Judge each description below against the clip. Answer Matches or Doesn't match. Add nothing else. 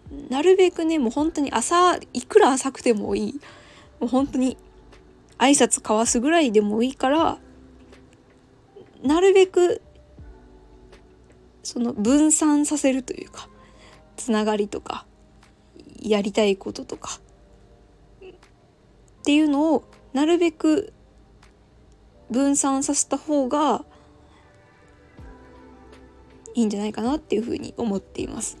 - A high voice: Matches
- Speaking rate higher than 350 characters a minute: Doesn't match